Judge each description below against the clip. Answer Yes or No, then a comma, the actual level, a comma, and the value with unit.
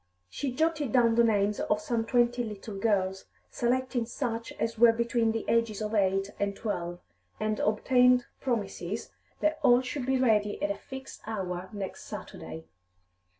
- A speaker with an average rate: Yes, average, 155 wpm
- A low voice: No, high, 225 Hz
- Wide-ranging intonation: No, average, 3.4 semitones